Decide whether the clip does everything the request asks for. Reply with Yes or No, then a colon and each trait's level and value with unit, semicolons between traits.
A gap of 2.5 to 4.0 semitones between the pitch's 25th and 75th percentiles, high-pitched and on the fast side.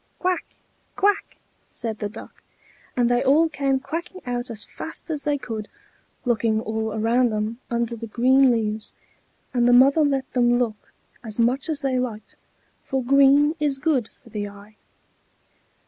No: average, 3.7 semitones; high, 245 Hz; average, 160 wpm